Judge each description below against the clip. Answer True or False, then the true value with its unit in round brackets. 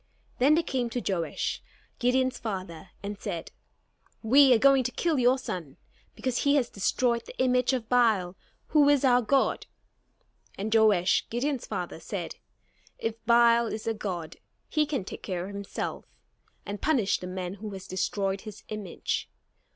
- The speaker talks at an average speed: True (160 wpm)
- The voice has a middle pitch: False (225 Hz)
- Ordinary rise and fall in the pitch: True (4.8 semitones)